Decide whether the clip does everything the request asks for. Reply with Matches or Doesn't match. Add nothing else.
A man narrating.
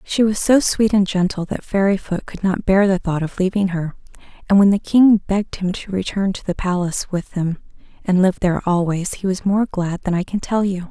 Doesn't match